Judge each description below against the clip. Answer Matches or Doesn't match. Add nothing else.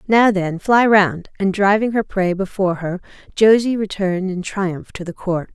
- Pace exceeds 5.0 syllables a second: Doesn't match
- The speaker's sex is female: Matches